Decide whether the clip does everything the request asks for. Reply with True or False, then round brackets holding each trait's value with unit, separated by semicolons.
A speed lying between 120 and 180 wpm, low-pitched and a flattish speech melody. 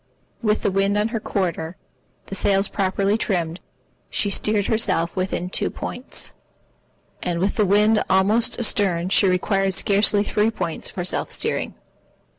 False (150 wpm; 195 Hz; 2.3 semitones)